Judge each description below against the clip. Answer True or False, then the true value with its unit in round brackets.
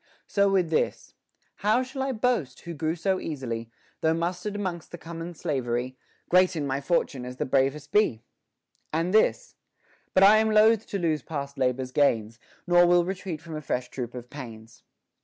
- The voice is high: False (165 Hz)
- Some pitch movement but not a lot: False (6.5 semitones)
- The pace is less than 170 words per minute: False (180 wpm)